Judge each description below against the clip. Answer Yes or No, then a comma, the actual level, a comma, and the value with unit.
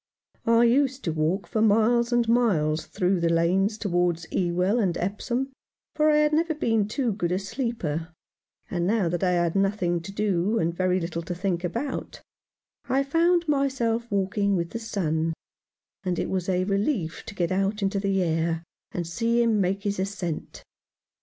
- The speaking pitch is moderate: No, high, 195 Hz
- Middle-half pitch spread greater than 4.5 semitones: Yes, average, 4.9 semitones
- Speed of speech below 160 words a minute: No, average, 175 wpm